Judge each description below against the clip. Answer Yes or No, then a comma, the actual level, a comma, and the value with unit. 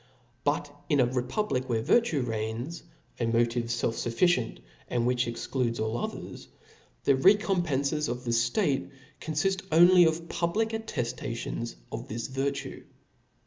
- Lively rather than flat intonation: Yes, wide, 6.2 semitones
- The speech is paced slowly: Yes, slow, 130 wpm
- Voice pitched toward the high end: No, low, 130 Hz